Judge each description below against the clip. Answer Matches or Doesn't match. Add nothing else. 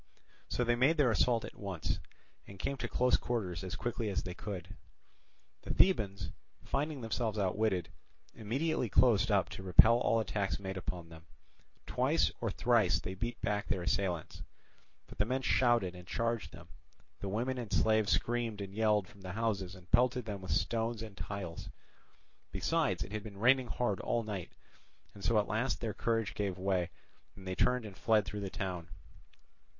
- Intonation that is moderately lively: Matches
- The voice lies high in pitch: Doesn't match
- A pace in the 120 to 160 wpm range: Doesn't match